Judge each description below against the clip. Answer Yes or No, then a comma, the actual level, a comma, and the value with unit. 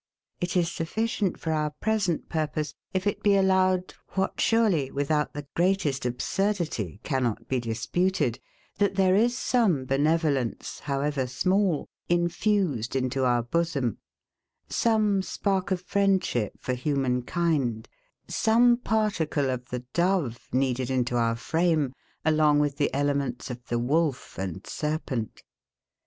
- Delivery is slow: Yes, slow, 130 wpm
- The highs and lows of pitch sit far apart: Yes, wide, 6.5 semitones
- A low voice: No, medium, 155 Hz